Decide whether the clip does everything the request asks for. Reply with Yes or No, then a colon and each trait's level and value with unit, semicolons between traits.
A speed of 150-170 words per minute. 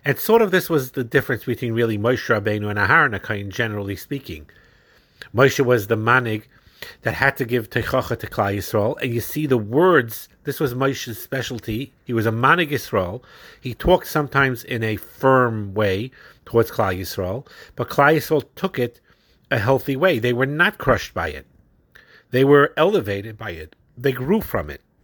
No: average, 180 wpm